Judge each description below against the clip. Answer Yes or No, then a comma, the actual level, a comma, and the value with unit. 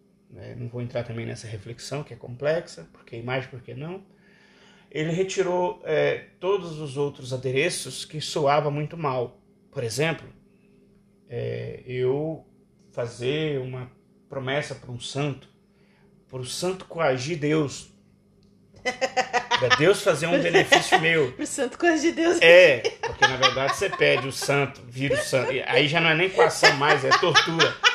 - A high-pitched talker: No, medium, 150 Hz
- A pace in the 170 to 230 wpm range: No, average, 150 wpm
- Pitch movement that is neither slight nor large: No, wide, 7.0 semitones